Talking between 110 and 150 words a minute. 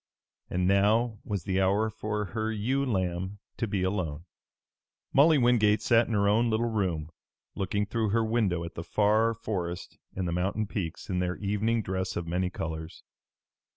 No: average, 170 wpm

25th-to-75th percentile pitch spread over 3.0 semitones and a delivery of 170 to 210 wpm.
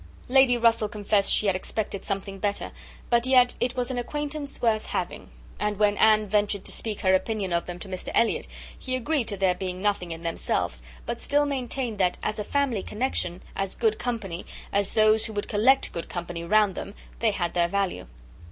Yes: average, 3.8 semitones; average, 200 wpm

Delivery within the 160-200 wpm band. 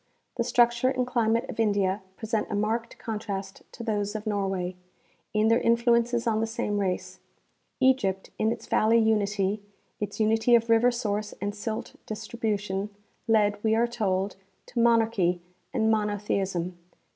No: average, 150 wpm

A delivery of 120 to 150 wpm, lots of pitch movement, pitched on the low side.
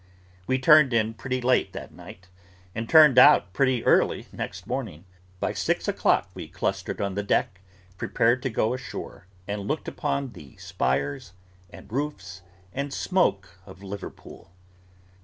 Yes: average, 145 wpm; wide, 5.7 semitones; low, 115 Hz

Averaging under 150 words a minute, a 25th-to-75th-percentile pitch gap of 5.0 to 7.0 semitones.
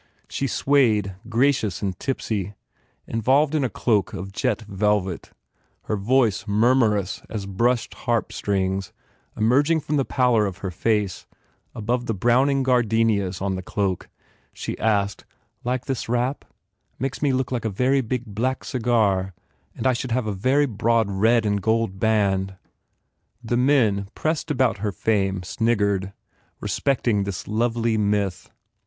No: average, 140 wpm; average, 4.1 semitones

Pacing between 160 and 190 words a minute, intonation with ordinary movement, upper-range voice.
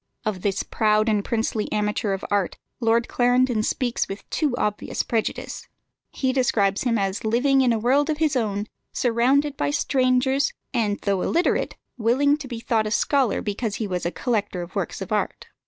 Yes: average, 180 wpm; average, 3.8 semitones; high, 230 Hz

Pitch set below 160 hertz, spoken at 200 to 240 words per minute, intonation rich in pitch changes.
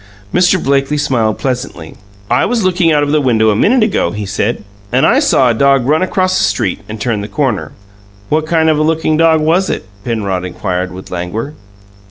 Yes: low, 135 Hz; fast, 205 wpm; wide, 6.8 semitones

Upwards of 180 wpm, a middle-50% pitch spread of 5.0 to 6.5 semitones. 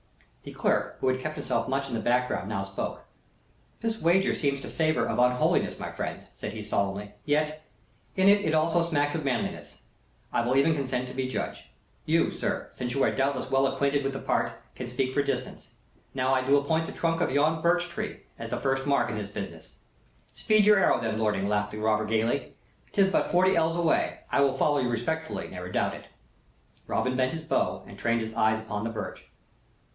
Yes: fast, 205 wpm; wide, 5.5 semitones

